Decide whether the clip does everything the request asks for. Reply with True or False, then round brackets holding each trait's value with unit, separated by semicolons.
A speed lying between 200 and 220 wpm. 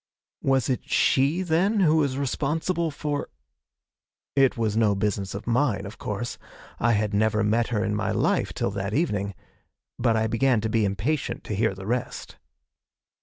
False (170 wpm)